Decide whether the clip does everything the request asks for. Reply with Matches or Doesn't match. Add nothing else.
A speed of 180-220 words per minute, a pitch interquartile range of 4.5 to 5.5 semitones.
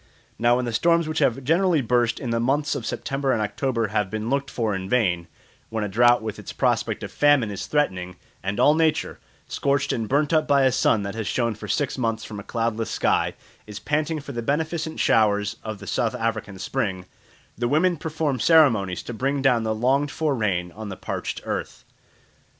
Matches